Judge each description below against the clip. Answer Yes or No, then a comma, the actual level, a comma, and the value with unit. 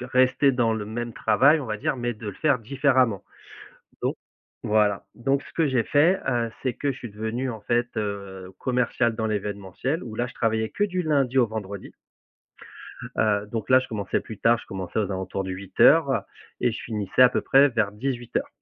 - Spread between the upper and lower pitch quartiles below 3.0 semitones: No, average, 3.8 semitones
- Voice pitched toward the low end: Yes, low, 115 Hz